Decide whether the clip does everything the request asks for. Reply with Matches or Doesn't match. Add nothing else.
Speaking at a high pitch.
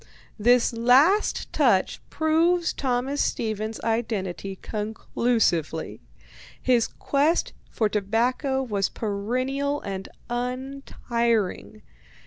Matches